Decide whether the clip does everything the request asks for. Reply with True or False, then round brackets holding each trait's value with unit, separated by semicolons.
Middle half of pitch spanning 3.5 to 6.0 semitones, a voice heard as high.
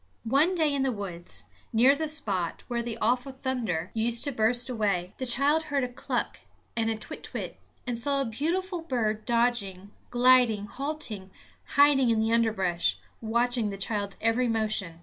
True (3.8 semitones; 235 Hz)